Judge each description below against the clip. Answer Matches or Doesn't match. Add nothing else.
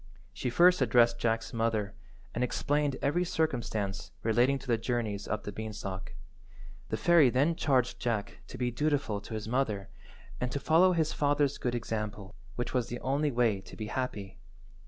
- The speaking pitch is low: Matches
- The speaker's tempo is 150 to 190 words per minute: Matches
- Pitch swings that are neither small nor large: Matches